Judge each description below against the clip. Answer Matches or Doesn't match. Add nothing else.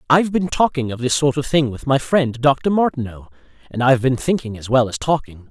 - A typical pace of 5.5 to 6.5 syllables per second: Matches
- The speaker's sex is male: Matches